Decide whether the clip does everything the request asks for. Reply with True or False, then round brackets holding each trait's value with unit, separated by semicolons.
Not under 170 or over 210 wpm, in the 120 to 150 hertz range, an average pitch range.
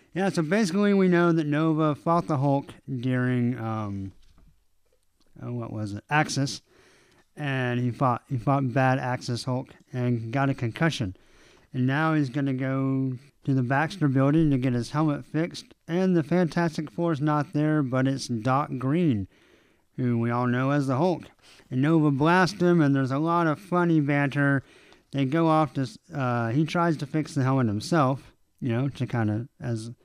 True (175 wpm; 135 Hz; 4.2 semitones)